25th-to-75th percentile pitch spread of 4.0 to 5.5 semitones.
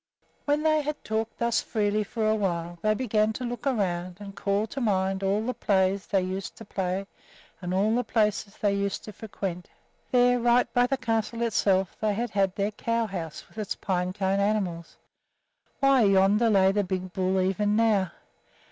No: average, 3.0 semitones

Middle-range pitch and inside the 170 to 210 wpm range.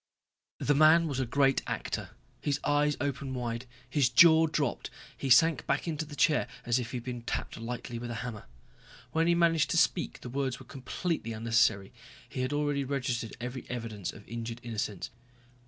No: low, 130 Hz; average, 185 wpm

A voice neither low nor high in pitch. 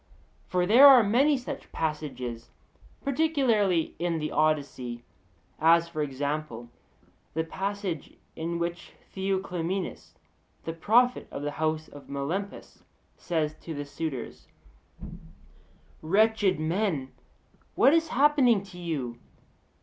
Yes: medium, 170 Hz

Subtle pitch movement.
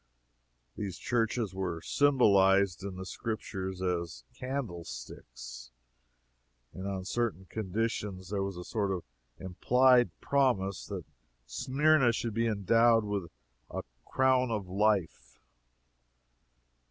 No: average, 4.0 semitones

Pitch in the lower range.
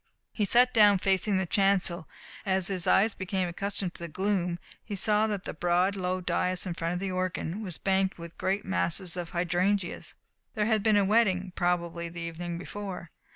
No: medium, 185 Hz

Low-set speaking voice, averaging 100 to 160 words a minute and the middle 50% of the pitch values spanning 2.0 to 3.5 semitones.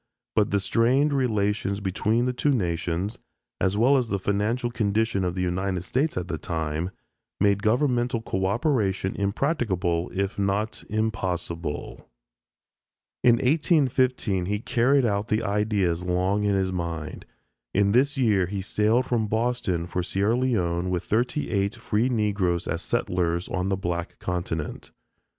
No: low, 100 Hz; average, 140 wpm; average, 4.5 semitones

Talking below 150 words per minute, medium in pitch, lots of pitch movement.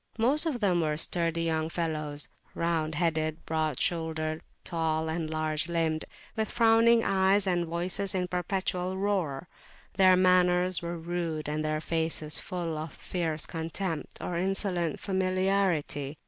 No: average, 140 wpm; medium, 170 Hz; average, 2.9 semitones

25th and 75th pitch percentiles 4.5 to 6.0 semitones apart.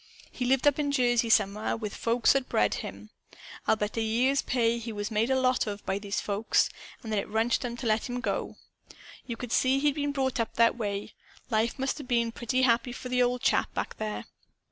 No: average, 2.8 semitones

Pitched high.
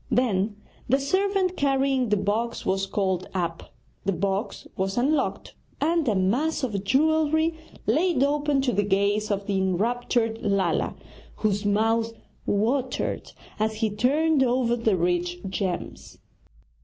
Yes: high, 225 Hz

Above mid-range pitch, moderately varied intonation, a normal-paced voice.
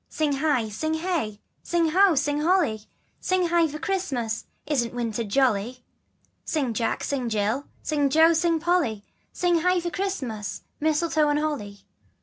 No: very high, 295 Hz; wide, 6.4 semitones; average, 145 wpm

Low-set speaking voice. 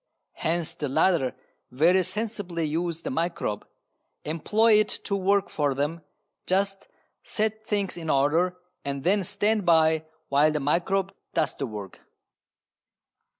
No: medium, 170 Hz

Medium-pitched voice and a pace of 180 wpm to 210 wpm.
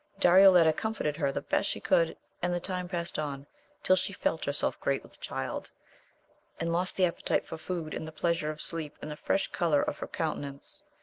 Yes: medium, 165 Hz; fast, 205 wpm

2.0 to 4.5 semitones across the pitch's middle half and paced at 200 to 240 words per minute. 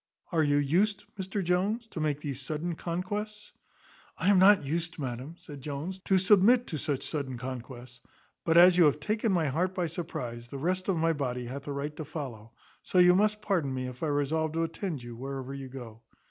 No: average, 5.2 semitones; fast, 205 wpm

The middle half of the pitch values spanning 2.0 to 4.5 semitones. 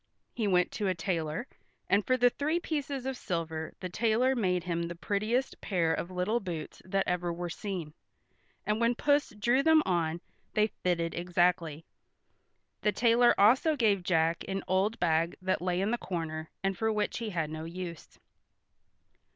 No: average, 5.1 semitones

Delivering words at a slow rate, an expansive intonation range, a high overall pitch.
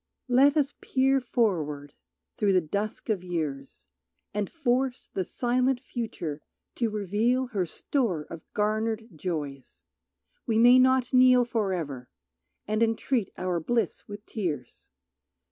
Yes: slow, 130 wpm; wide, 6.1 semitones; high, 215 Hz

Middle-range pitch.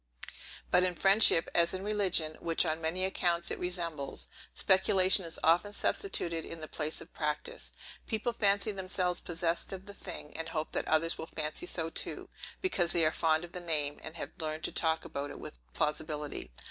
Yes: medium, 170 Hz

